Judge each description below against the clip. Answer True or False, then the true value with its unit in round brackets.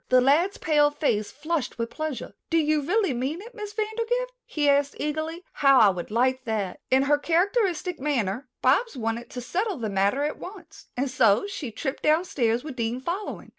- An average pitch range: False (5.7 semitones)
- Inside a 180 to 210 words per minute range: True (185 wpm)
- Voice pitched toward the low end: False (290 Hz)